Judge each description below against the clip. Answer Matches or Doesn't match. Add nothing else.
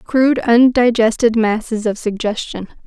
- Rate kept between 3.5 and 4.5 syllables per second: Doesn't match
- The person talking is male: Doesn't match